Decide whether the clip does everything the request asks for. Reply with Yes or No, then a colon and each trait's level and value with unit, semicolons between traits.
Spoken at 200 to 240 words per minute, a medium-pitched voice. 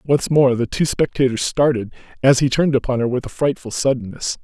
No: fast, 205 wpm; low, 130 Hz